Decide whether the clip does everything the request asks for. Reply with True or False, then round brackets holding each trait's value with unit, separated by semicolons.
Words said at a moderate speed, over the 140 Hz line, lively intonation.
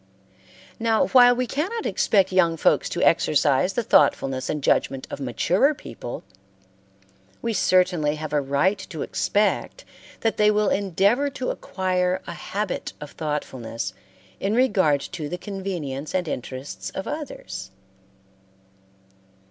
False (130 wpm; 185 Hz; 6.3 semitones)